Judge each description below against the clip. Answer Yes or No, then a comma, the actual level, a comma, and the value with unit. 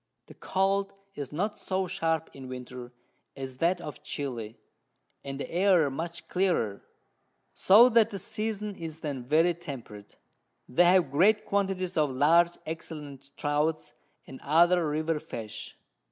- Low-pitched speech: No, medium, 160 Hz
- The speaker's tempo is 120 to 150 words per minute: Yes, average, 140 wpm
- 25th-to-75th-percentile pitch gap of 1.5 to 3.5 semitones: No, average, 5.1 semitones